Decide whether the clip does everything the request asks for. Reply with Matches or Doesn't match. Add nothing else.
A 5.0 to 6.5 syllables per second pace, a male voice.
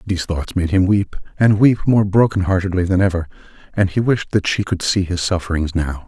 Matches